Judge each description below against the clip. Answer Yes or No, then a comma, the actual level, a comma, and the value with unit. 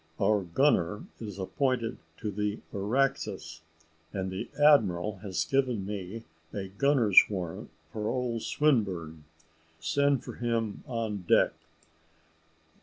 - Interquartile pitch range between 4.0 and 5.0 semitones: Yes, average, 4.7 semitones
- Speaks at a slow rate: Yes, slow, 110 wpm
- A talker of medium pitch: No, low, 105 Hz